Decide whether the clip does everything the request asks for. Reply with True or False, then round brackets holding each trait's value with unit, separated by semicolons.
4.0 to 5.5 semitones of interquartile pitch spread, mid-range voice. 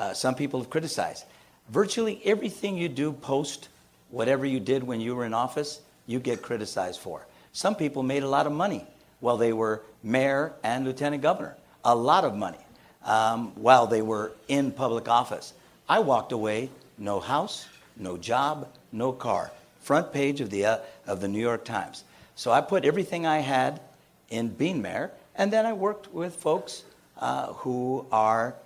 False (4.6 semitones; 130 Hz)